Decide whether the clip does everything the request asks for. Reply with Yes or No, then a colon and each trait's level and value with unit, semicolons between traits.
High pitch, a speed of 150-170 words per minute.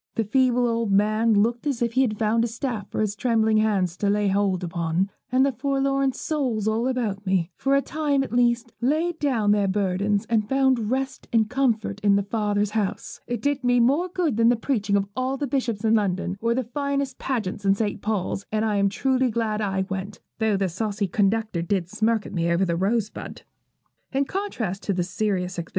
No: high, 220 Hz; average, 195 wpm